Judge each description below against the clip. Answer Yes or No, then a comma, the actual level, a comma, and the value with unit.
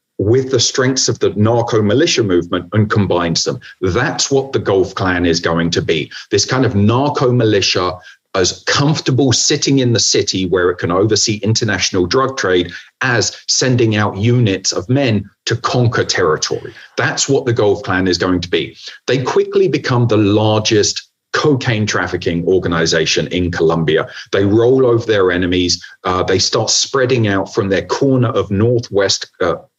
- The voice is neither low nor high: No, low, 110 Hz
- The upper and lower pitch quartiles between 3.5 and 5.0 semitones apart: Yes, average, 4.7 semitones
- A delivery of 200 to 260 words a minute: No, average, 165 wpm